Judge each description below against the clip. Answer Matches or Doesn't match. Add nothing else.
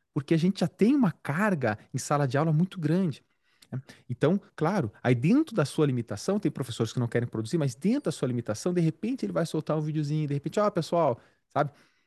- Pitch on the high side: Doesn't match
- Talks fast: Matches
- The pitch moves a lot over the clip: Matches